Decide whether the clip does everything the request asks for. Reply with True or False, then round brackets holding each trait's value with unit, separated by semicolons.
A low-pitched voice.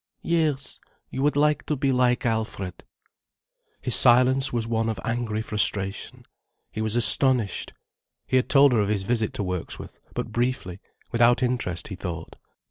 True (120 Hz)